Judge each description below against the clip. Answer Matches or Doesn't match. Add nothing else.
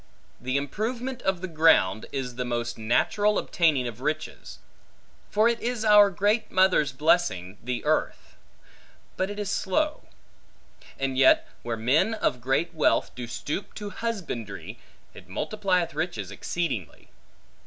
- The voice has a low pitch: Doesn't match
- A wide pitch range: Matches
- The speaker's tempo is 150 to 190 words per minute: Doesn't match